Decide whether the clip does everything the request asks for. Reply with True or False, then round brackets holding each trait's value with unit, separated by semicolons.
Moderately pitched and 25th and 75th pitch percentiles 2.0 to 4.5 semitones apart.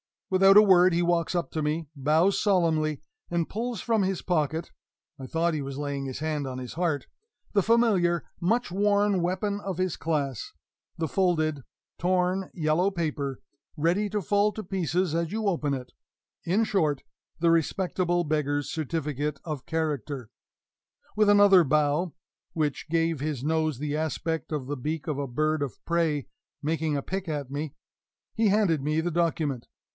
True (165 Hz; 3.9 semitones)